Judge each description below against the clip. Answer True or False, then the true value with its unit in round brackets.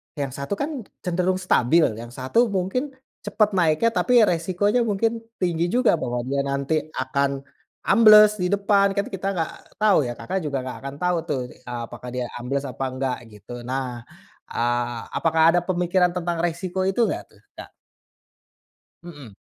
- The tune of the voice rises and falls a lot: True (6.7 semitones)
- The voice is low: False (170 Hz)